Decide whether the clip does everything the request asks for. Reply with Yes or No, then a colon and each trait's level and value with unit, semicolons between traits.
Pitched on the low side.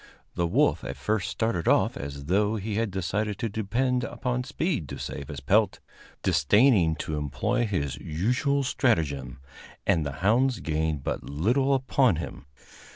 Yes: low, 100 Hz